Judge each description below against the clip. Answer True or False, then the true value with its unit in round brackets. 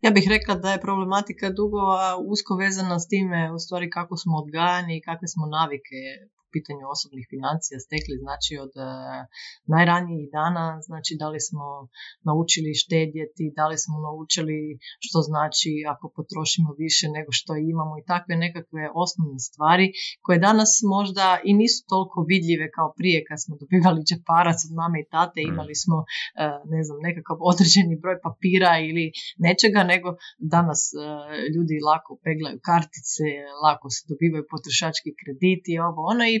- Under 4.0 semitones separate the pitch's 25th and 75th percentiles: True (2.7 semitones)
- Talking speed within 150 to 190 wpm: True (155 wpm)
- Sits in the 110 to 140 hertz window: False (160 Hz)